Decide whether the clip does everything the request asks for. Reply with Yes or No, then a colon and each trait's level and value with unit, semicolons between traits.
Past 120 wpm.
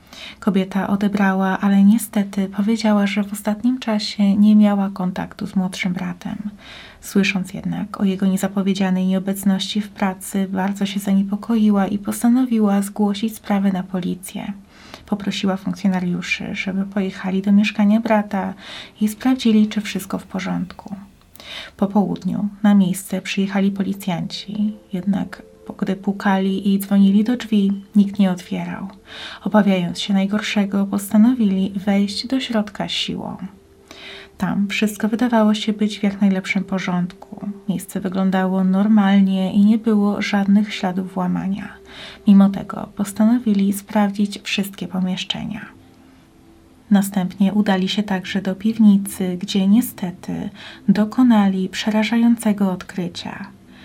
No: average, 115 wpm